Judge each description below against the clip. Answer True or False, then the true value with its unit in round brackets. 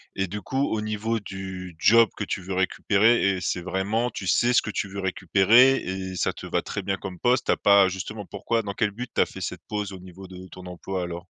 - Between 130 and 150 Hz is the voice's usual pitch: False (95 Hz)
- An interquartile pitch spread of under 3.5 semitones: True (2.5 semitones)